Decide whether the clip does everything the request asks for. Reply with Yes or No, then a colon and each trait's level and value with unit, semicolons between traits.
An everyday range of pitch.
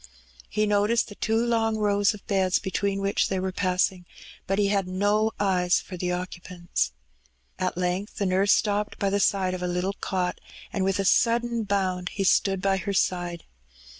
No: narrow, 1.9 semitones